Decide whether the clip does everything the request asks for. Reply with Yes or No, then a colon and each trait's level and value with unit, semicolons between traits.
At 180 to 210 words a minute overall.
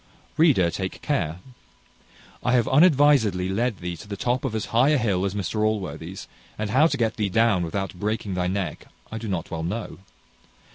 Yes: average, 190 wpm